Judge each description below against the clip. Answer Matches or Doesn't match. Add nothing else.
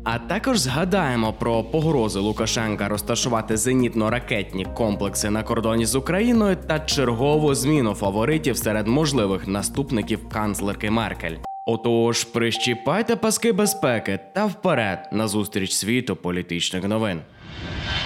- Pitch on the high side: Doesn't match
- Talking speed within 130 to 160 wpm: Doesn't match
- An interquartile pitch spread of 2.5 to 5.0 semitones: Doesn't match